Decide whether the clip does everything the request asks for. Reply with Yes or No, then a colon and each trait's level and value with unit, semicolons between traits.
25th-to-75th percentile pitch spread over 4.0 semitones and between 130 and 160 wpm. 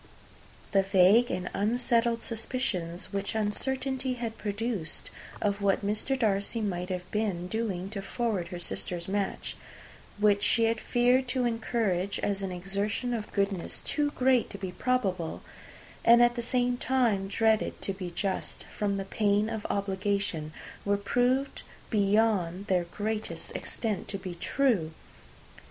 No: average, 3.4 semitones; average, 140 wpm